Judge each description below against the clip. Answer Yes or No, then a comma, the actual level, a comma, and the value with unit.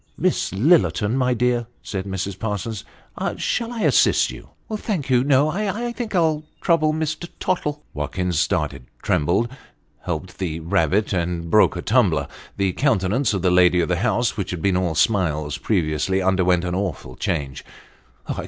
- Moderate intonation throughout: No, wide, 7.2 semitones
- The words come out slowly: No, average, 170 wpm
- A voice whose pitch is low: Yes, very low, 95 Hz